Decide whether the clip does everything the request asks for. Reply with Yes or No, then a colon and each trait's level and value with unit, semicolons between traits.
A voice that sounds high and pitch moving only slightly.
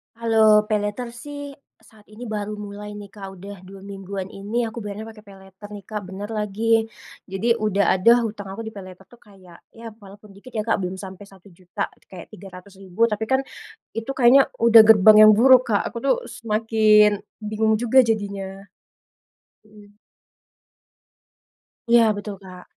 Yes: high, 205 Hz; narrow, 2.2 semitones